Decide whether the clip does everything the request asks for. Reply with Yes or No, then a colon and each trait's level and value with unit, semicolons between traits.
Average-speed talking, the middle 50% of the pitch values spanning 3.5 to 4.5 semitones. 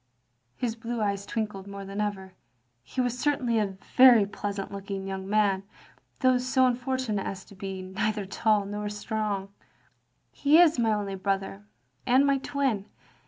Yes: average, 160 wpm; average, 3.9 semitones